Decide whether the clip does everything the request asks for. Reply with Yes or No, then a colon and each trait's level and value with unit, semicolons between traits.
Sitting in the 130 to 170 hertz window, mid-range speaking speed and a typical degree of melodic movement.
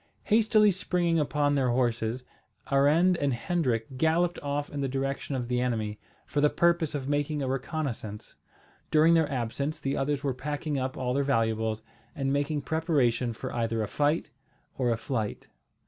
Yes: medium, 140 Hz; average, 165 wpm; average, 3.8 semitones